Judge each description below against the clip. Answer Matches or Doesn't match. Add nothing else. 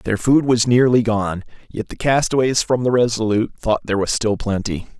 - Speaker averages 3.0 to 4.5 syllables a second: Doesn't match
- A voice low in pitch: Matches